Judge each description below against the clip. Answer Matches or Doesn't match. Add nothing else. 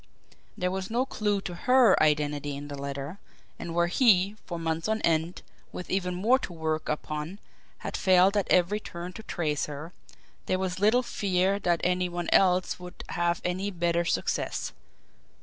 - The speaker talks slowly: Doesn't match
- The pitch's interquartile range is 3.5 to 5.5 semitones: Doesn't match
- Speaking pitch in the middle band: Matches